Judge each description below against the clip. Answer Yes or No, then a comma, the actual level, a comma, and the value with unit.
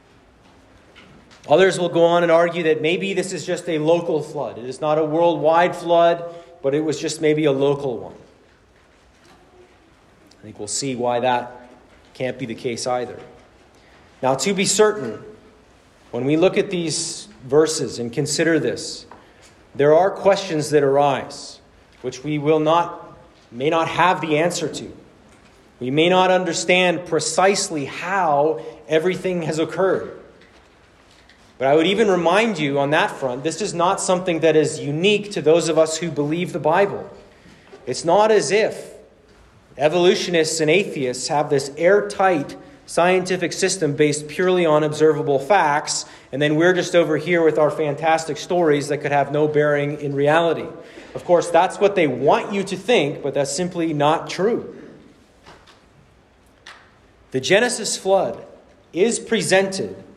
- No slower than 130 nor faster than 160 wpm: Yes, average, 155 wpm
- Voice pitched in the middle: Yes, medium, 160 Hz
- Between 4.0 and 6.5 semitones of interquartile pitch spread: No, average, 3.4 semitones